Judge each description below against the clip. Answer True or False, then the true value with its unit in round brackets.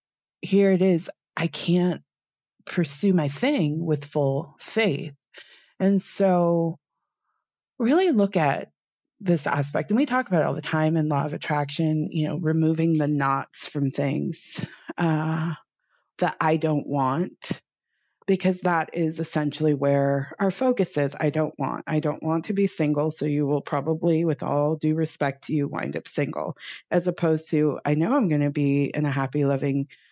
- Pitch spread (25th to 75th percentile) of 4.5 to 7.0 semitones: False (3.3 semitones)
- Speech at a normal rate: True (165 wpm)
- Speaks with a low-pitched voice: False (155 Hz)